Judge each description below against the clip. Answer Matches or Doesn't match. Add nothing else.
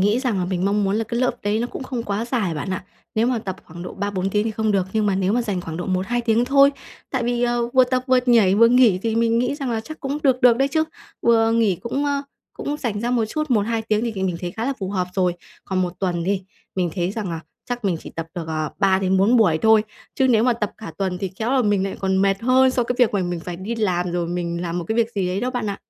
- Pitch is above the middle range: Matches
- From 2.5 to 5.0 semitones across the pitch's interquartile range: Matches